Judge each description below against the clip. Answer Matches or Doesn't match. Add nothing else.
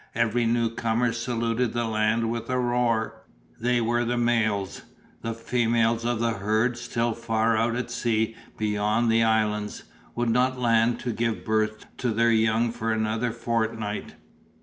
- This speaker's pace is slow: Doesn't match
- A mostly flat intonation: Matches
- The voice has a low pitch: Matches